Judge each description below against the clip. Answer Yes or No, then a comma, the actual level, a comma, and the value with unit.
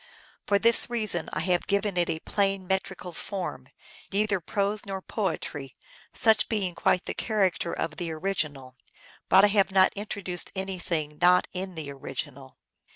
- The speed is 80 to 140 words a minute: No, average, 160 wpm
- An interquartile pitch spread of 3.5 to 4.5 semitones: No, average, 2.7 semitones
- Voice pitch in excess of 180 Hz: Yes, high, 190 Hz